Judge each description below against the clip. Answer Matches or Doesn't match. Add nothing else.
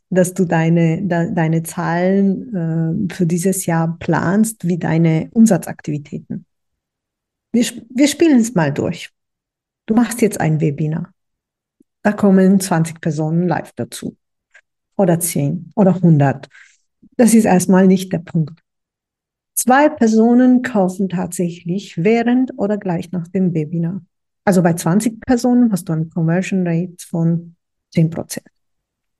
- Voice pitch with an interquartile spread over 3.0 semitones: Matches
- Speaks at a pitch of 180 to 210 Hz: Matches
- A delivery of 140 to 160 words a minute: Doesn't match